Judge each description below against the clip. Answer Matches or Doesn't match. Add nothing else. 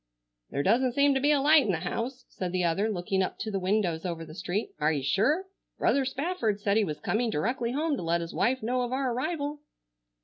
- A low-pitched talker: Doesn't match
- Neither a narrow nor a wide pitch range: Doesn't match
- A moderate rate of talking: Doesn't match